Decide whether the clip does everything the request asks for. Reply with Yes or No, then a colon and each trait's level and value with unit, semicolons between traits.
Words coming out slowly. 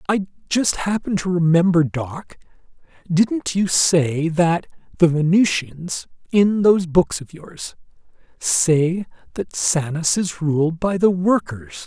Yes: slow, 125 wpm